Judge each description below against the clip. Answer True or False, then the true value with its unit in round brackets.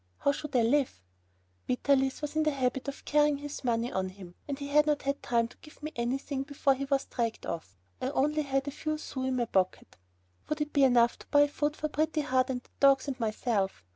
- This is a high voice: True (275 Hz)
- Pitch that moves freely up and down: False (3.2 semitones)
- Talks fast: True (230 wpm)